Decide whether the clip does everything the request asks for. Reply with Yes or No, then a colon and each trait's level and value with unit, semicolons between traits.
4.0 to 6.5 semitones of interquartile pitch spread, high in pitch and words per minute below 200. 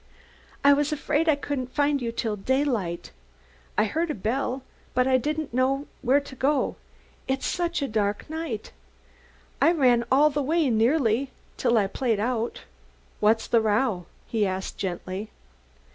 Yes: average, 4.7 semitones; very high, 255 Hz; average, 155 wpm